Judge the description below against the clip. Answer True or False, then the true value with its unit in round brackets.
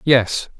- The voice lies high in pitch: False (125 Hz)